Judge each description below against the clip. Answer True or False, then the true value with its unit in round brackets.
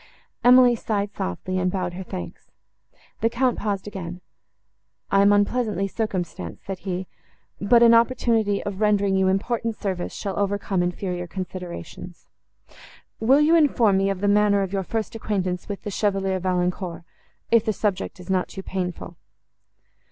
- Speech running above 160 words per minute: False (150 wpm)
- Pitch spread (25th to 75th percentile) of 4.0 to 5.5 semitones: False (2.8 semitones)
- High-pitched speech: True (195 Hz)